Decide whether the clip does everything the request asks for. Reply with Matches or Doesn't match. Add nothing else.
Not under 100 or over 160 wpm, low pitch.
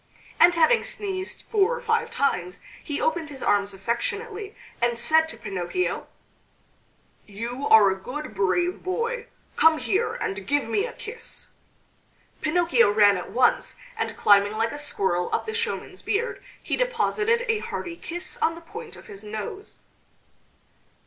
Doesn't match